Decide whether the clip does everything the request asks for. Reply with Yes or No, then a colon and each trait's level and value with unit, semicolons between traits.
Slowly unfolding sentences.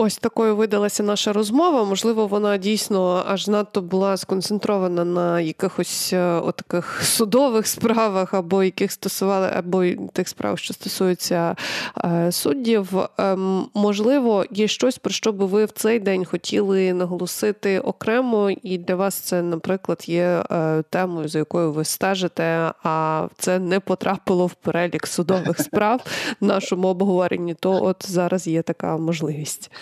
No: average, 135 wpm